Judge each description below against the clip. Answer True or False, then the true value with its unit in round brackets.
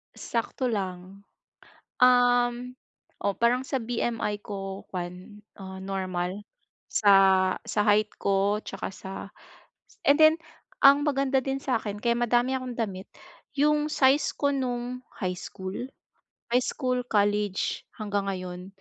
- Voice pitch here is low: False (215 Hz)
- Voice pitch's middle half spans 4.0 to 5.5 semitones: True (4.5 semitones)